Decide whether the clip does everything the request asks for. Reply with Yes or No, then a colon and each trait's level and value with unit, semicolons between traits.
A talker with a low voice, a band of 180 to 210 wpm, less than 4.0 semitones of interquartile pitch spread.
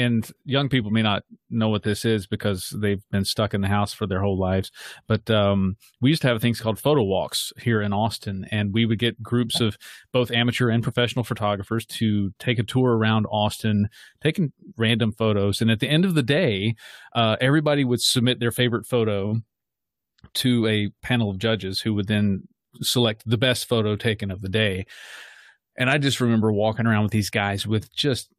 Yes: low, 110 Hz; average, 200 wpm; average, 2.8 semitones